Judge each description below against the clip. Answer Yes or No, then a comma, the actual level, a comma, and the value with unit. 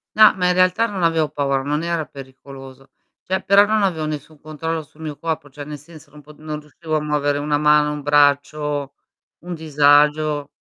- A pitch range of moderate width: No, narrow, 2.0 semitones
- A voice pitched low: No, medium, 150 Hz